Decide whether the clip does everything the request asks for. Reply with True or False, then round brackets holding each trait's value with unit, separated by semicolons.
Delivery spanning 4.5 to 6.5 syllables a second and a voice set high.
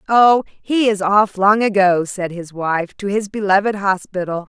False (4.2 syllables/s; 200 Hz)